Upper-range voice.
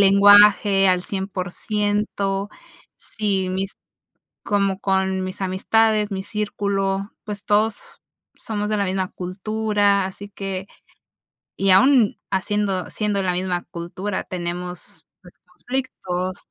Yes: high, 195 Hz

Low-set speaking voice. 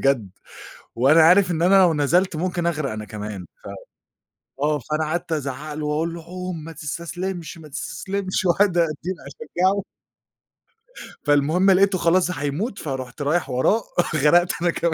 No: medium, 165 Hz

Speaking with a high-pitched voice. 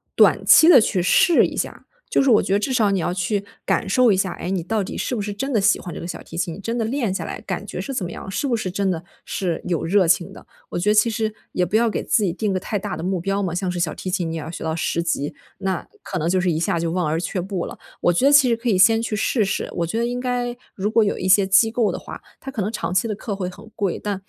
Yes: high, 195 Hz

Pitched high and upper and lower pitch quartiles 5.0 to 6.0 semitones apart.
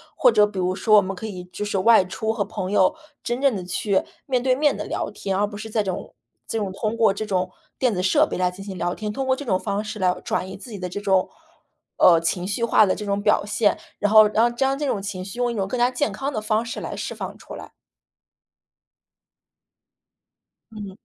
No: high, 210 Hz; average, 3.4 semitones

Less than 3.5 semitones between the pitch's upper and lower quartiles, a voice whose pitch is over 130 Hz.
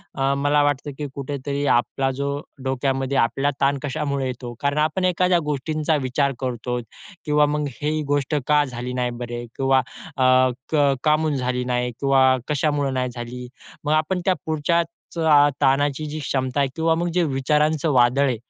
Yes: narrow, 2.5 semitones; medium, 140 Hz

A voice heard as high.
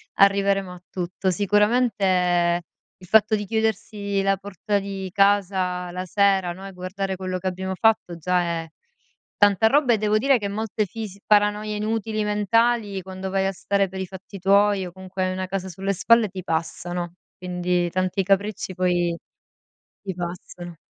Yes: high, 195 Hz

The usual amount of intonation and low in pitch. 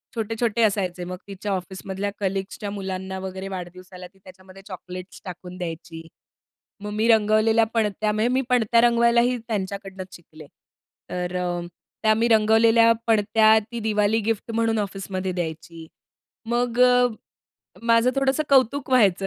No: average, 3.5 semitones; high, 205 Hz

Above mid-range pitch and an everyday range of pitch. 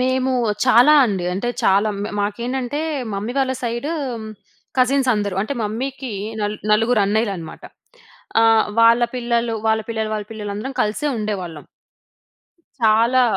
Yes: high, 225 Hz; average, 3.2 semitones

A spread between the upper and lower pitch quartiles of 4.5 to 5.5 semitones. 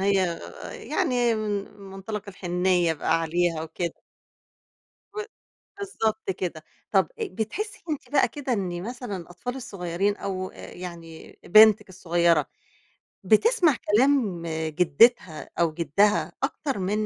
Yes: average, 4.8 semitones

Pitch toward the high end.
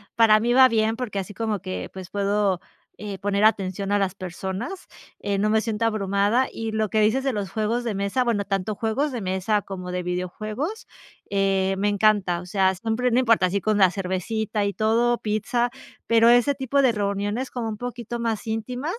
Yes: high, 215 Hz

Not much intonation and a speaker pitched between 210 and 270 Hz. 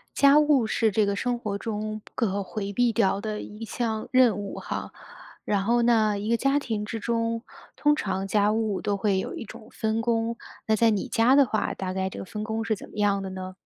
Yes: narrow, 2.3 semitones; high, 215 Hz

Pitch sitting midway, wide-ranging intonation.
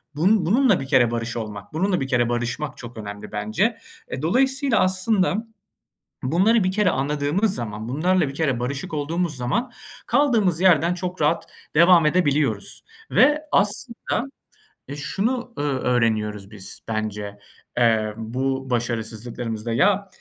Yes: medium, 145 Hz; wide, 8.1 semitones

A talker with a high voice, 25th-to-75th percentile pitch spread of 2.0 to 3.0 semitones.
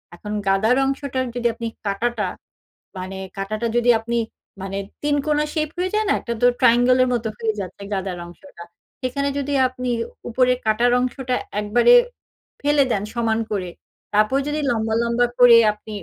No: high, 235 Hz; average, 3.5 semitones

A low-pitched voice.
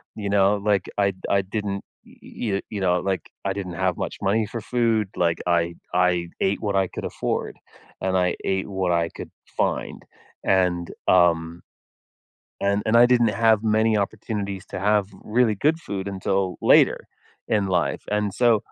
Yes: low, 100 Hz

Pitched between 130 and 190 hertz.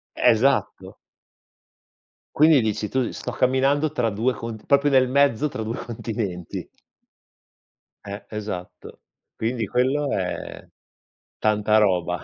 No: low, 115 Hz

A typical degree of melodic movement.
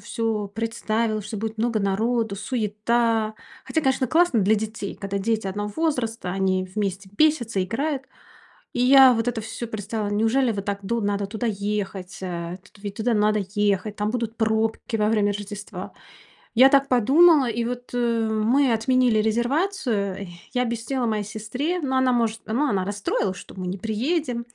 Yes: average, 3.0 semitones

